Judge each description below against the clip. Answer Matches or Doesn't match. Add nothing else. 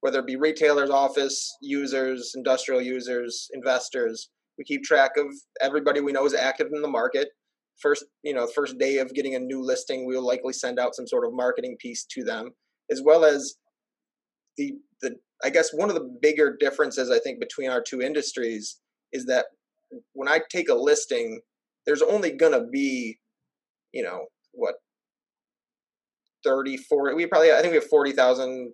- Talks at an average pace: Matches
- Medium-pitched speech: Matches